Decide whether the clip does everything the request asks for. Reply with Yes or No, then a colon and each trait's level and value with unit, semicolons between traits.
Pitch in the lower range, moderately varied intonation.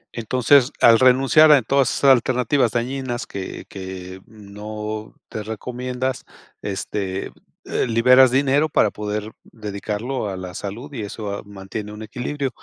Yes: low, 115 Hz; average, 3.9 semitones